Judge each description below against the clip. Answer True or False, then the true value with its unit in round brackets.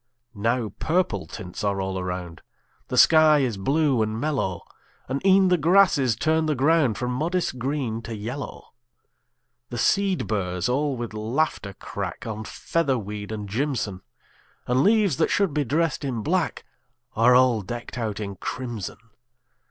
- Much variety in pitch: True (6.2 semitones)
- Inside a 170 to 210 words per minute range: False (150 wpm)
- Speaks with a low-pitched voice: True (125 Hz)